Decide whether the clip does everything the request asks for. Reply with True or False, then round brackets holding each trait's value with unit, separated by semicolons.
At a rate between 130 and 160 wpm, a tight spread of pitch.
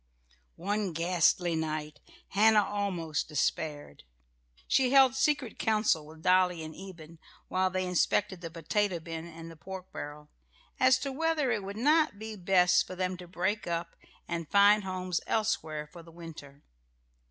False (155 wpm; 4.1 semitones)